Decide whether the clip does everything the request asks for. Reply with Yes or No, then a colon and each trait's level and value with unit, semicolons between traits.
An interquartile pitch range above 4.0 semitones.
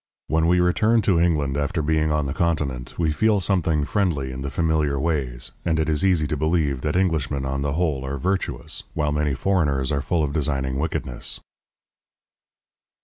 No: average, 3.3 semitones